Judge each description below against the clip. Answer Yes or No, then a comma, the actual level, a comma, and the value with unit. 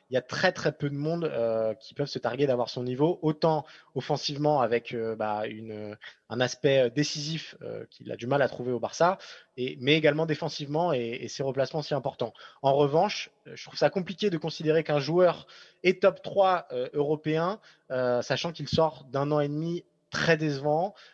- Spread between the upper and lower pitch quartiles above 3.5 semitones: Yes, average, 4.0 semitones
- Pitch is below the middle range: No, medium, 150 Hz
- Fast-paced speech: No, average, 195 wpm